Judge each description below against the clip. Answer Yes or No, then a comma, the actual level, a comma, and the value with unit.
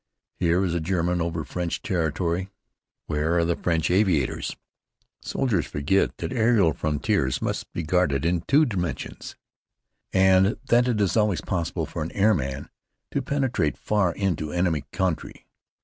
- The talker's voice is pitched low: Yes, very low, 90 Hz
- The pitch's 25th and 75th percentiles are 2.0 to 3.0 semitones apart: No, average, 3.4 semitones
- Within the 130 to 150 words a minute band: Yes, average, 145 wpm